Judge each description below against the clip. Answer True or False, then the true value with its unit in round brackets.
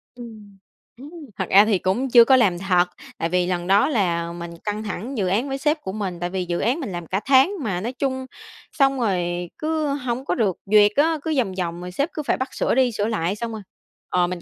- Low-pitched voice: False (210 Hz)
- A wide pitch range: True (6.4 semitones)